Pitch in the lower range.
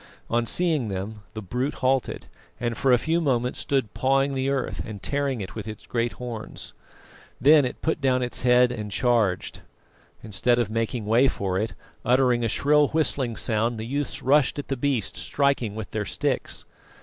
Yes: low, 125 Hz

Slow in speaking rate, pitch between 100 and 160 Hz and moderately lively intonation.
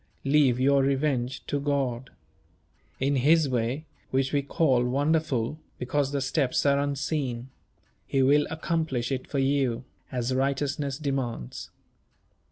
No: slow, 125 wpm; low, 135 Hz; narrow, 2.1 semitones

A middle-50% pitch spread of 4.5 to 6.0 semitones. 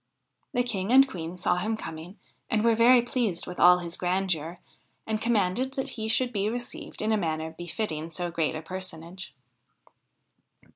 Yes: average, 5.1 semitones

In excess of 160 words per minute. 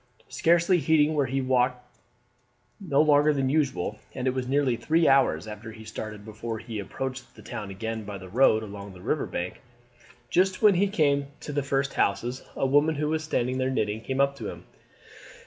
Yes: average, 200 wpm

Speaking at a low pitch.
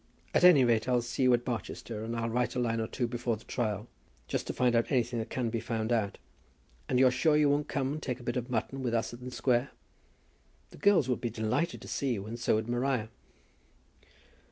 Yes: low, 120 Hz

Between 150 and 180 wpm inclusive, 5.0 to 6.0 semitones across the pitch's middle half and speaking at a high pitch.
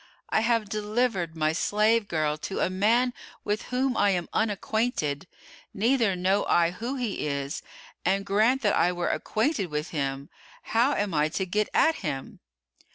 Yes: average, 160 wpm; average, 5.3 semitones; high, 200 Hz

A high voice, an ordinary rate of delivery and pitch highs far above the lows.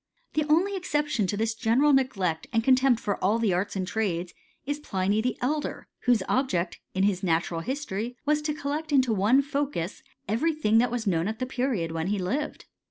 Yes: high, 230 Hz; average, 175 wpm; wide, 6.7 semitones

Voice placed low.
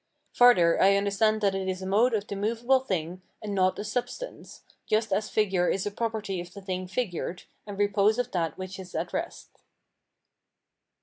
No: high, 200 Hz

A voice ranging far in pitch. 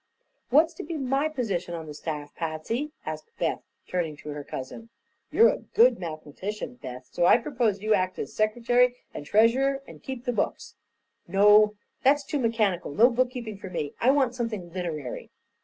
Yes: wide, 6.7 semitones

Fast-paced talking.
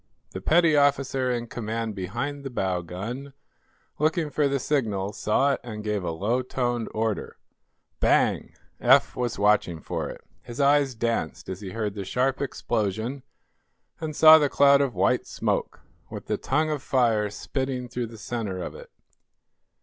No: average, 165 wpm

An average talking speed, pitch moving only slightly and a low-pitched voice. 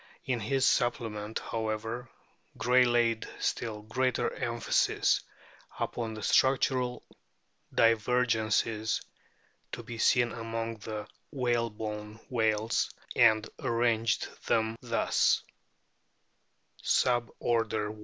No: slow, 95 wpm; narrow, 1.8 semitones; low, 115 Hz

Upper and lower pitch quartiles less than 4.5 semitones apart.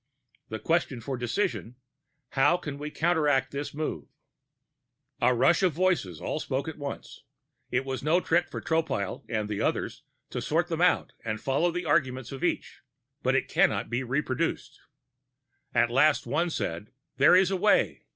No: average, 5.2 semitones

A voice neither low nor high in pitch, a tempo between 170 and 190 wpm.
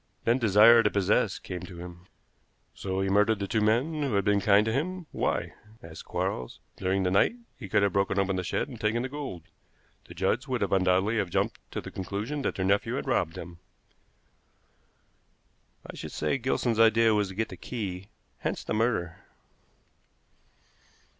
No: low, 105 Hz; average, 180 wpm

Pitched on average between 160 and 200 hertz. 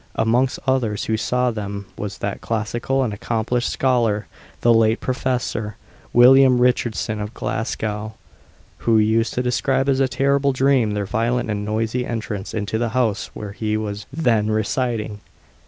No: low, 115 Hz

